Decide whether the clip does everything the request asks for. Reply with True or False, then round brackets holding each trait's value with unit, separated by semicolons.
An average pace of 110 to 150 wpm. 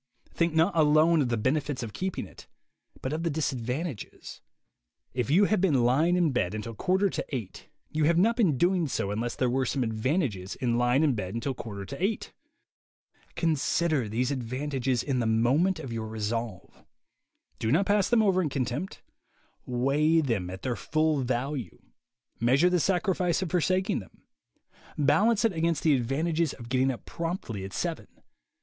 False (175 wpm)